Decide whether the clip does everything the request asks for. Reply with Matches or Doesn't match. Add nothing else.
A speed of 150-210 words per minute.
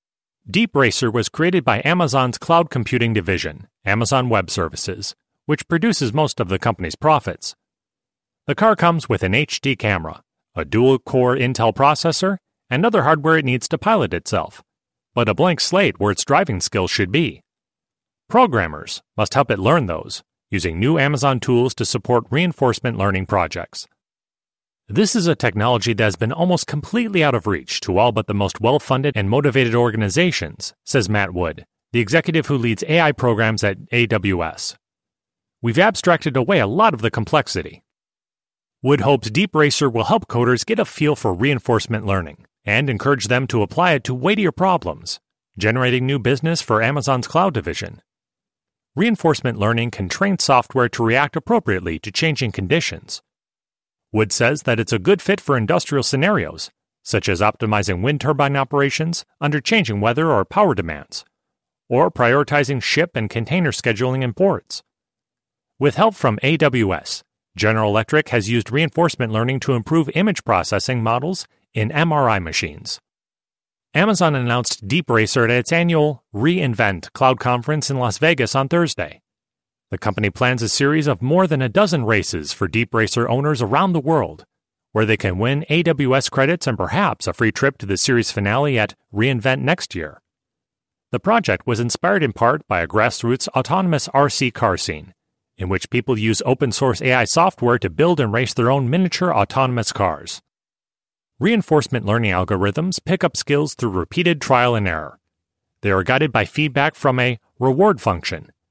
Matches